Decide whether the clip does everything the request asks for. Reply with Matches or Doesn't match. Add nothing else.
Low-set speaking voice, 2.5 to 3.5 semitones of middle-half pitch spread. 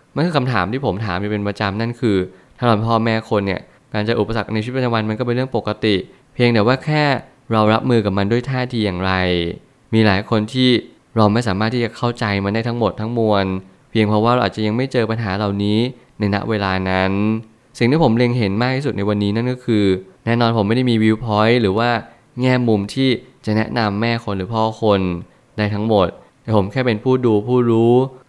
Matches